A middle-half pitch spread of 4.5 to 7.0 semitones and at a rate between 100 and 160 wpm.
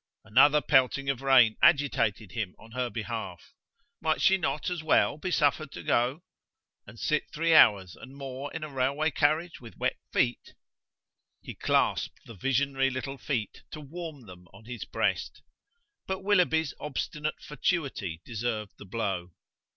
Yes: average, 5.2 semitones; average, 150 wpm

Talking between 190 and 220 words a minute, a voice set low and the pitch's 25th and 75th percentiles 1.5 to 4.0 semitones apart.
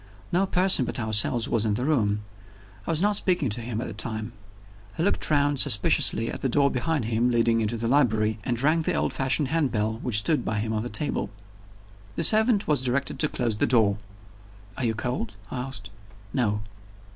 No: average, 200 wpm; low, 120 Hz; average, 4.7 semitones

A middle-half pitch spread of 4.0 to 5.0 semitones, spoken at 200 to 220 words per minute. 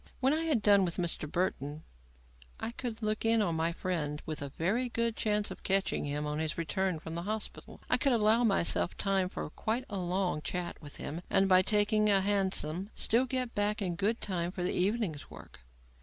Yes: average, 4.3 semitones; fast, 205 wpm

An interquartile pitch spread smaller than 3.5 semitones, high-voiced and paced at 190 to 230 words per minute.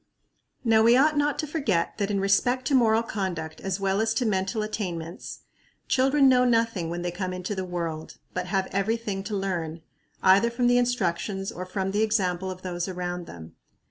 No: average, 4.2 semitones; high, 195 Hz; average, 195 wpm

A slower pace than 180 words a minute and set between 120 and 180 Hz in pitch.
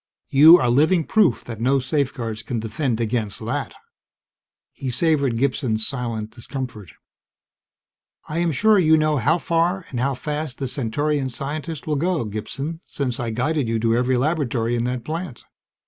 Yes: average, 160 wpm; low, 135 Hz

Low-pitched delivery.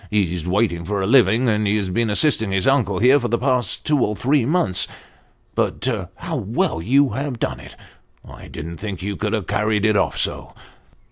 Yes: low, 105 Hz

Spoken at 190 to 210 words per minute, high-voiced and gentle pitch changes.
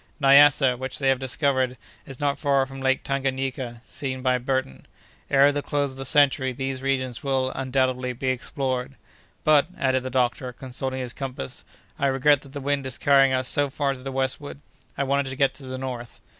No: average, 195 wpm; low, 135 Hz; narrow, 1.2 semitones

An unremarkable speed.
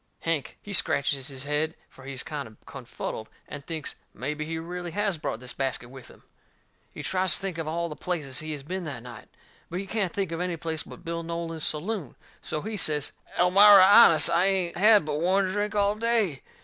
No: fast, 210 wpm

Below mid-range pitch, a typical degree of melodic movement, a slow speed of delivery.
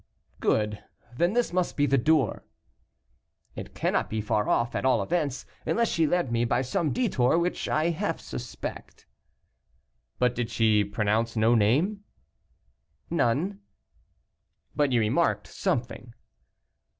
No: low, 130 Hz; wide, 6.8 semitones; slow, 130 wpm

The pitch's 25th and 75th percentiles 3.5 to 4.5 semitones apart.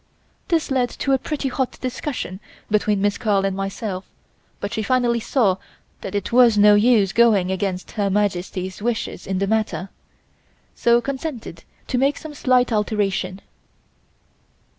Yes: average, 4.2 semitones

